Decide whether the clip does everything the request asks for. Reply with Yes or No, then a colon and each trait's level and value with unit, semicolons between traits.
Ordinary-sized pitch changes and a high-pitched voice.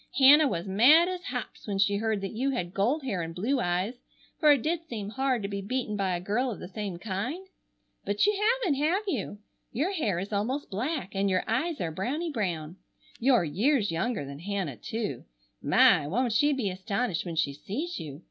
No: wide, 6.3 semitones; high, 215 Hz